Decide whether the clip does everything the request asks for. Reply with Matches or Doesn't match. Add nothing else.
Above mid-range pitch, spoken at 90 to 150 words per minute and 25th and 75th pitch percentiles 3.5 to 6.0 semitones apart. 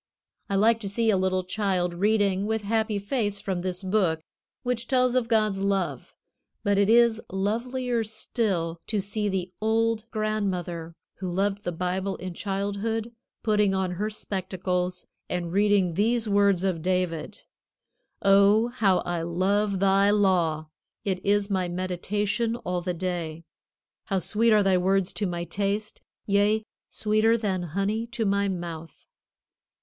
Doesn't match